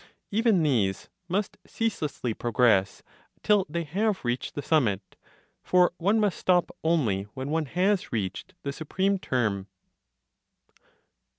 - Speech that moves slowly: Yes, slow, 120 wpm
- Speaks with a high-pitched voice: No, medium, 155 Hz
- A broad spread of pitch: Yes, wide, 7.9 semitones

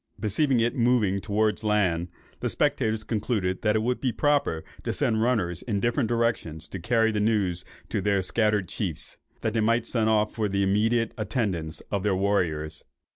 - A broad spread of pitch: No, average, 3.3 semitones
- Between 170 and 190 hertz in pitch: No, low, 105 Hz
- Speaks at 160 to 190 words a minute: Yes, average, 180 wpm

